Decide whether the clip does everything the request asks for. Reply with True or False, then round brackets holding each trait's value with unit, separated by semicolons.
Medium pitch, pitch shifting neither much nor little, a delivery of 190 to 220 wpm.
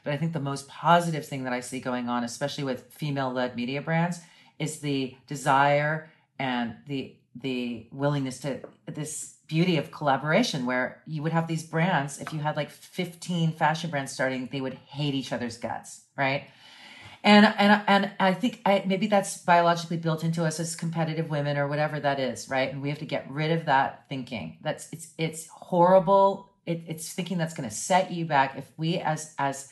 True (150 Hz; 3.6 semitones; 195 wpm)